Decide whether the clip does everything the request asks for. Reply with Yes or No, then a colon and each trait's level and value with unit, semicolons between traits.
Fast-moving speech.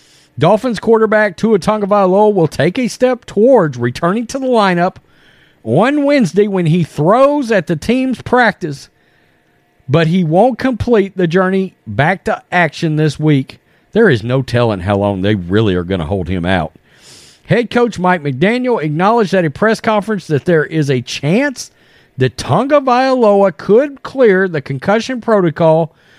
No: average, 155 wpm